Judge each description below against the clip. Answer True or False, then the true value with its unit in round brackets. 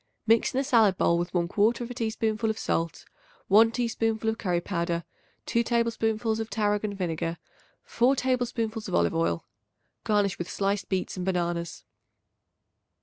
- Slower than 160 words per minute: True (145 wpm)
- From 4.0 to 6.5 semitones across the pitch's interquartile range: True (4.4 semitones)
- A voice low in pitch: False (215 Hz)